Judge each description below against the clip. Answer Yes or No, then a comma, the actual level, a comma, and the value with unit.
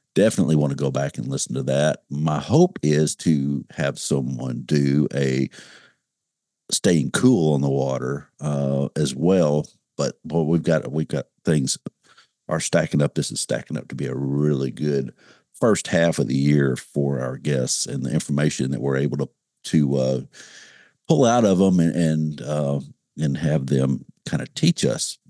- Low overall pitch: Yes, very low, 70 Hz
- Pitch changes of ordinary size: No, narrow, 2.1 semitones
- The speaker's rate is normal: Yes, average, 180 wpm